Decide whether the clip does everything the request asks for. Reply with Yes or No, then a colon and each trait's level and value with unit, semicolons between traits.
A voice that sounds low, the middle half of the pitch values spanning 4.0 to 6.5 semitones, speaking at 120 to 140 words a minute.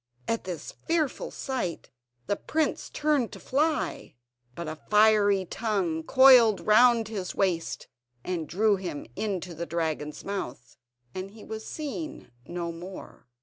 No: high, 200 Hz; average, 5.3 semitones; slow, 135 wpm